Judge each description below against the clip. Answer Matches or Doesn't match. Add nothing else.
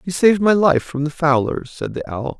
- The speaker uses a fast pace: Matches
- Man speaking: Matches